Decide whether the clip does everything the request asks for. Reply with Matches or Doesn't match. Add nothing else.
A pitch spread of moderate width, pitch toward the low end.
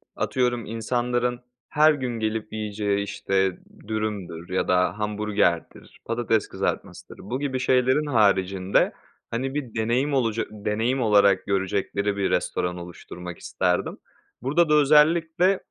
Matches